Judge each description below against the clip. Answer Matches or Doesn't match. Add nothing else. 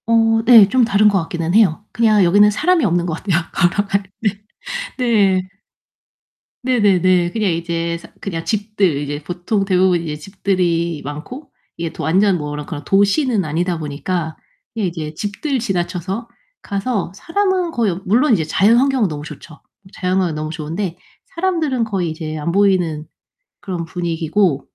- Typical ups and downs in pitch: Matches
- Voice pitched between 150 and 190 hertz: Matches